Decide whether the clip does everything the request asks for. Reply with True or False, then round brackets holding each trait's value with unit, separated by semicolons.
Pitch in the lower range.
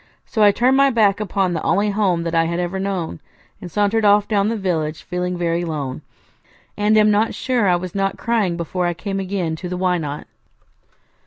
False (190 Hz)